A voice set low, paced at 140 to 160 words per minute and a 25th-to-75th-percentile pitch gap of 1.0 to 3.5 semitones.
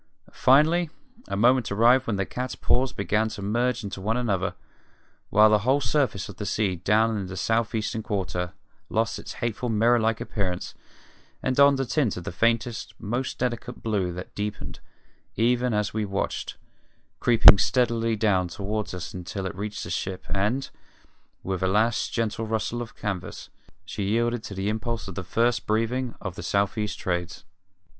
No: low, 110 Hz; average, 170 wpm; average, 3.2 semitones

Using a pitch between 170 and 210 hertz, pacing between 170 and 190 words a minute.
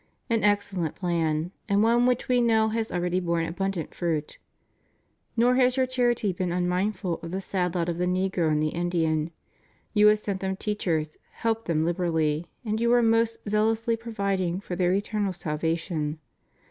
Yes: medium, 185 Hz; average, 175 wpm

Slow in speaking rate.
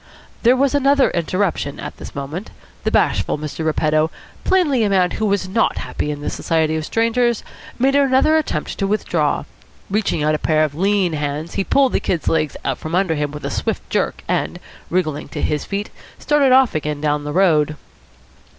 No: average, 185 wpm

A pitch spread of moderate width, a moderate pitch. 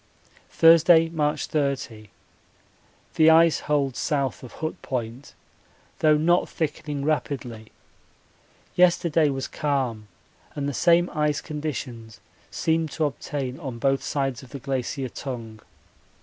Yes: average, 3.4 semitones; medium, 145 Hz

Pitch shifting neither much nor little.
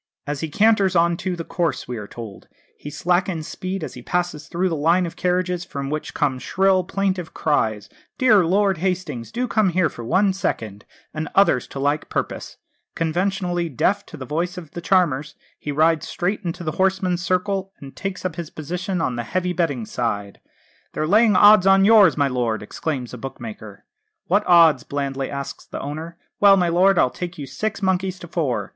Yes: average, 4.6 semitones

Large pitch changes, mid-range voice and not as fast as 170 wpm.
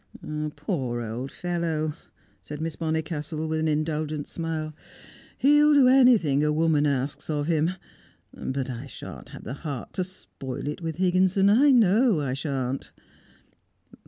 No: average, 3.7 semitones; medium, 155 Hz; average, 140 wpm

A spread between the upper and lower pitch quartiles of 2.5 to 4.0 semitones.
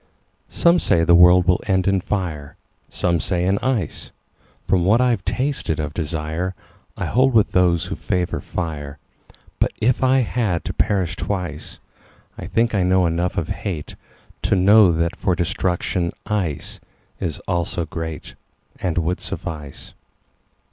Yes: average, 3.2 semitones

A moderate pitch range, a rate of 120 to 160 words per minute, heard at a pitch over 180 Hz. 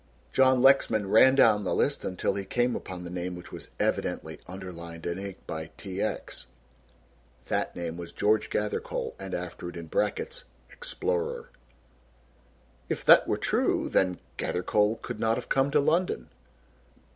No: average, 4.2 semitones; average, 155 wpm; very low, 95 Hz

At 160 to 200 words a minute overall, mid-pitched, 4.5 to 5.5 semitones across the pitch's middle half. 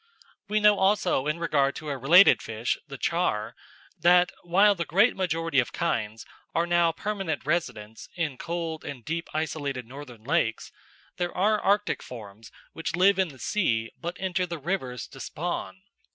Yes: average, 165 wpm; medium, 165 Hz; average, 5.1 semitones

